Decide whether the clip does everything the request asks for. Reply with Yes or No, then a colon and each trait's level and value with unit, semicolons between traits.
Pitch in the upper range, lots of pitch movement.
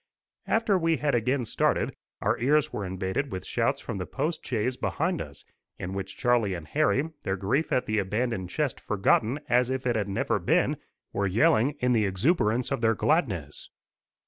No: low, 120 Hz; wide, 6.2 semitones